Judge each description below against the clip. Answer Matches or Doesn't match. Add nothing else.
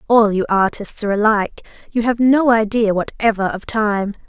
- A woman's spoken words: Matches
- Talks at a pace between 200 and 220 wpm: Doesn't match